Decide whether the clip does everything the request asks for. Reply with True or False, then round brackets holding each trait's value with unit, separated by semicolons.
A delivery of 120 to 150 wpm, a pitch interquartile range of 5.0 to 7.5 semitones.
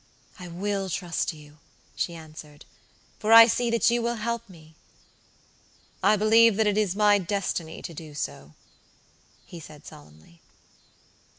True (140 wpm; 5.6 semitones)